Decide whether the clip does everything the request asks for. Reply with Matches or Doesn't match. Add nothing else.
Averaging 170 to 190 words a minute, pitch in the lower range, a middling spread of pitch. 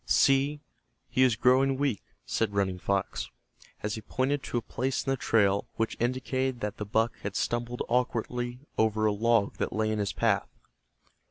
Matches